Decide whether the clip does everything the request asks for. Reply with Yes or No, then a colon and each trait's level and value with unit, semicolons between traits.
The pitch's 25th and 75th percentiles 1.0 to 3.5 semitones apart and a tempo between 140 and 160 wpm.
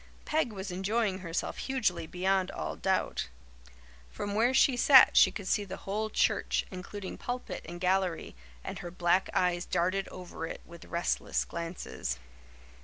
Yes: average, 3.0 semitones; average, 150 wpm